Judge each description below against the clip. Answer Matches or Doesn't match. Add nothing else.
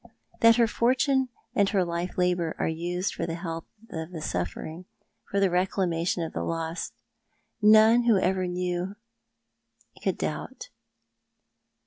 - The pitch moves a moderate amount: Matches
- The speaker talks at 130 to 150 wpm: Matches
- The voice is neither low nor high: Matches